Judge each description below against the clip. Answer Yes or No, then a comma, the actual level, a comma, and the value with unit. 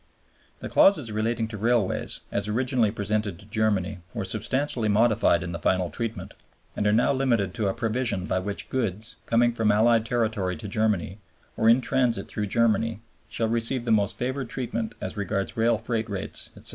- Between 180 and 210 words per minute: Yes, average, 185 wpm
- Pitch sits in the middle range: No, low, 110 Hz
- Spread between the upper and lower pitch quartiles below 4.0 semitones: Yes, narrow, 2.4 semitones